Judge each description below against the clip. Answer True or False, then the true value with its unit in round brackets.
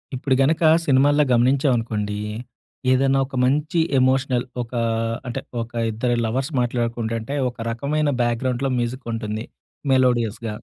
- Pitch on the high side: False (125 Hz)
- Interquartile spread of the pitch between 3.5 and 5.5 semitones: False (2.6 semitones)